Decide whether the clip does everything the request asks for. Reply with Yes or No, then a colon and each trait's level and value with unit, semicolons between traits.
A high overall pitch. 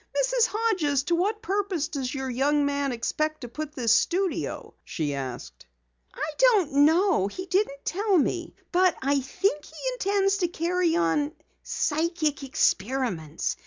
Yes: very high, 310 Hz